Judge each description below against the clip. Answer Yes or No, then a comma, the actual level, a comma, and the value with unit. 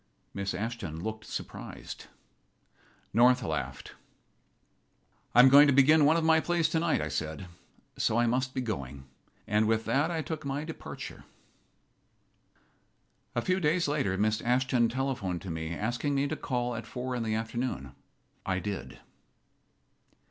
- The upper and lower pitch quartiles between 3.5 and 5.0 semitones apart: No, wide, 5.6 semitones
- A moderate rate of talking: Yes, average, 150 wpm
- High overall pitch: No, low, 120 Hz